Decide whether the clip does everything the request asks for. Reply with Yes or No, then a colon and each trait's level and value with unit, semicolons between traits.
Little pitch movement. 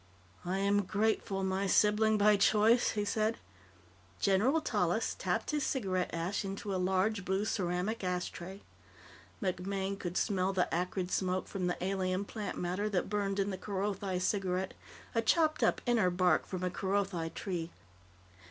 Yes: narrow, 2.2 semitones